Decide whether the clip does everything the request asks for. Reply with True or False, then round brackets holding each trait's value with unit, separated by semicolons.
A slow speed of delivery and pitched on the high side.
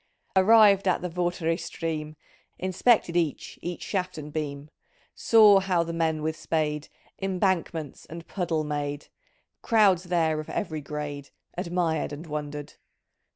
False (130 wpm; 165 Hz)